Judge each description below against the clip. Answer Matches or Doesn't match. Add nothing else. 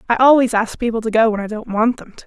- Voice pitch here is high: Matches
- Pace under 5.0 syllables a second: Doesn't match